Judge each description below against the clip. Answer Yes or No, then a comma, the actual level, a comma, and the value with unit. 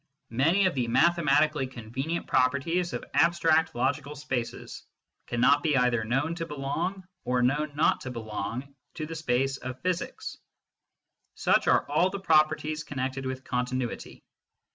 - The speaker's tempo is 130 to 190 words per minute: Yes, average, 140 wpm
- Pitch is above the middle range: No, medium, 140 Hz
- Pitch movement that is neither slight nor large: Yes, average, 3.9 semitones